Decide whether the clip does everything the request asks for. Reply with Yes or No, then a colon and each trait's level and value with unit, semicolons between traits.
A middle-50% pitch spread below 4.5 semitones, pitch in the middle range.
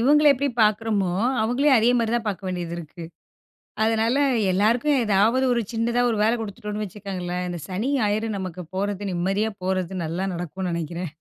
No: average, 3.7 semitones; high, 205 Hz